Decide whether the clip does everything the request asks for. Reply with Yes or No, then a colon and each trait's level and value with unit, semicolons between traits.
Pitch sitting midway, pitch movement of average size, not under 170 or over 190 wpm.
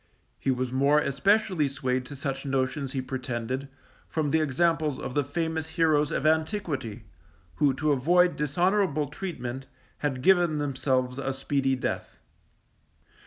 No: medium, 145 Hz; average, 3.5 semitones; slow, 135 wpm